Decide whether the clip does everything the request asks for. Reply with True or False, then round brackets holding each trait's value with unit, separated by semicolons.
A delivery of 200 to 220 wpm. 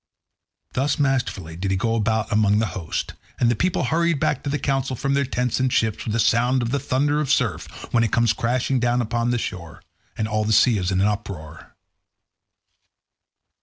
True (205 wpm)